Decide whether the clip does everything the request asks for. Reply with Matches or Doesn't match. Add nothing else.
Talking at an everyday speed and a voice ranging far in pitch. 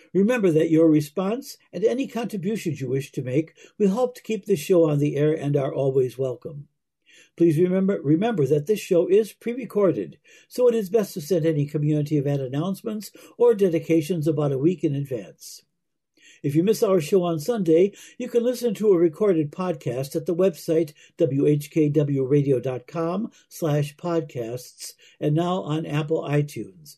Doesn't match